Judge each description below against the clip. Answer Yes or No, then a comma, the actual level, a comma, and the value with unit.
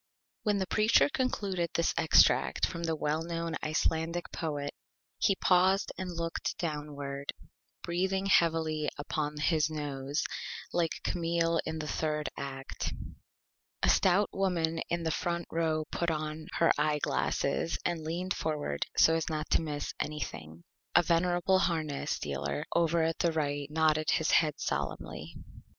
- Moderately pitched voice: Yes, medium, 160 Hz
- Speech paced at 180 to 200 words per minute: No, average, 140 wpm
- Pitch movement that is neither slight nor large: No, narrow, 2.3 semitones